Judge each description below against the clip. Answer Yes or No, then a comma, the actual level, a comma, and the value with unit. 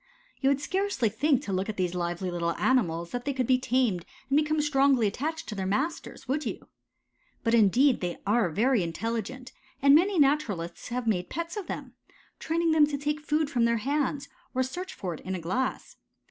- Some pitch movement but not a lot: No, wide, 6.9 semitones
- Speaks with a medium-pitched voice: No, very high, 255 Hz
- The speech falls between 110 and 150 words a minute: No, average, 200 wpm